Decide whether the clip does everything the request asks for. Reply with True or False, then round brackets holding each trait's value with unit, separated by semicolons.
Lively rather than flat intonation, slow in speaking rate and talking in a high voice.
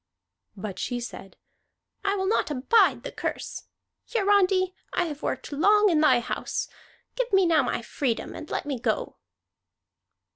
False (7.1 semitones; 150 wpm; 335 Hz)